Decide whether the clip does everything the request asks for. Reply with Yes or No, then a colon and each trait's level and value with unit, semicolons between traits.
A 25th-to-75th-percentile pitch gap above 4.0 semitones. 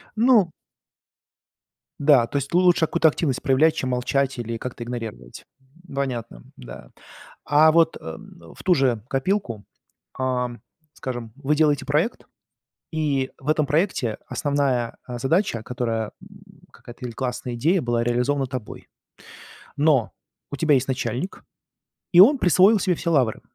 Yes: average, 4.6 semitones